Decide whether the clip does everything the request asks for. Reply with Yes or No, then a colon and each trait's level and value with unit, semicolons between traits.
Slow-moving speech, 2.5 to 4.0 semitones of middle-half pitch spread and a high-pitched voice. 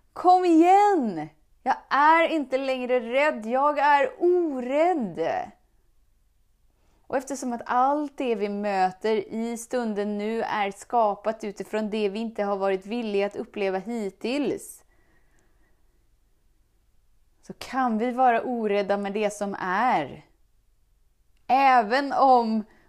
No: slow, 115 wpm; average, 5.2 semitones; high, 235 Hz